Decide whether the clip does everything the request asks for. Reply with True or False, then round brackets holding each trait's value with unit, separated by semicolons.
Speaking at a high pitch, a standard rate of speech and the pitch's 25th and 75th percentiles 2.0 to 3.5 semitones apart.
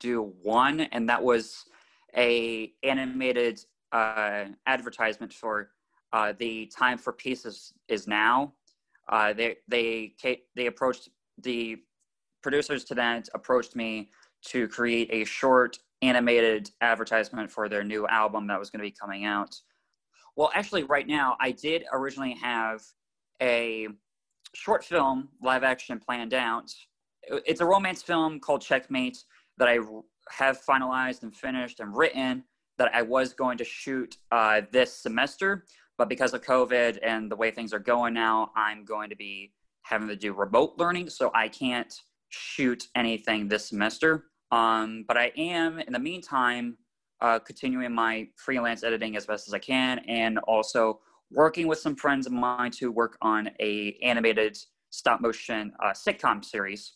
False (120 Hz; 155 wpm; 2.9 semitones)